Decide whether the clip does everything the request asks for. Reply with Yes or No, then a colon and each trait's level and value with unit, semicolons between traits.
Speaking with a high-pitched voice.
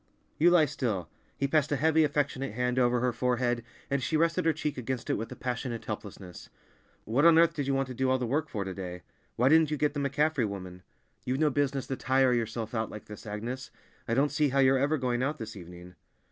No: low, 130 Hz